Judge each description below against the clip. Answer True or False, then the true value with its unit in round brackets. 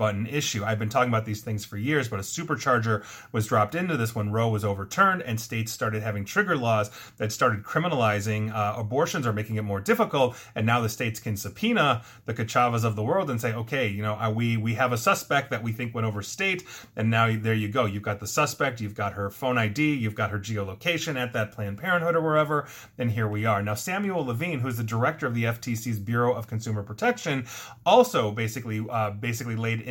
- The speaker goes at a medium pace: False (225 wpm)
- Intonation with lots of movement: False (3.3 semitones)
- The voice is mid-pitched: False (115 Hz)